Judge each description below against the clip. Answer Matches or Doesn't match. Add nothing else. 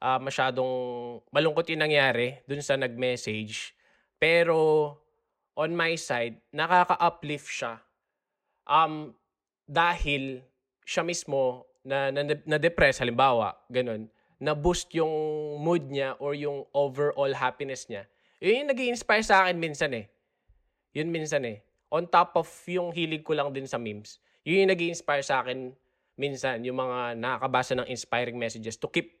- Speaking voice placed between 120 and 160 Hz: Matches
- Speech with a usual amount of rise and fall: Matches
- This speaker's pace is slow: Doesn't match